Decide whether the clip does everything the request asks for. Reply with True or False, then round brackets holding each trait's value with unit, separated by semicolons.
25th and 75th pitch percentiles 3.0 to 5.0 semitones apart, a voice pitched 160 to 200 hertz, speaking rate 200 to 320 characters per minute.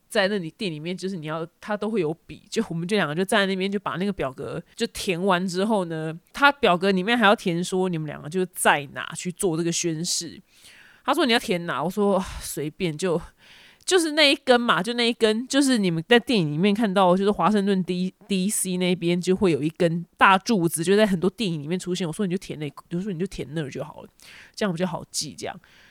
False (3.5 semitones; 185 Hz; 335 characters per minute)